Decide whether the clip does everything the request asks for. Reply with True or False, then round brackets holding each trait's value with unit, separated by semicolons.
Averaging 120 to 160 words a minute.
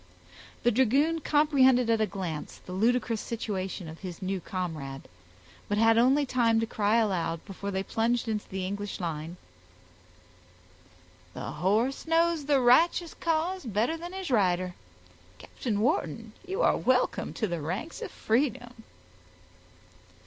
True (140 wpm)